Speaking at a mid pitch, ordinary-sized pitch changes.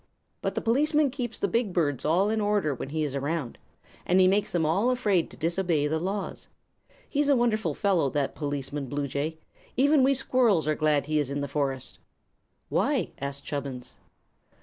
No: medium, 165 Hz; wide, 7.1 semitones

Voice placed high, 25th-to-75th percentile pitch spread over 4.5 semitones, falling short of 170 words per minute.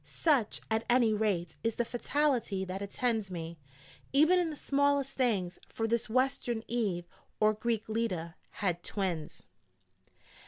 Yes: high, 220 Hz; average, 4.9 semitones; average, 140 wpm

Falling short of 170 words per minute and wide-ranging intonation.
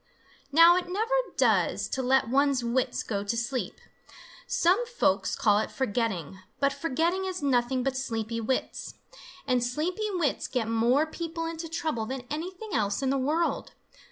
Yes: average, 155 wpm; wide, 5.9 semitones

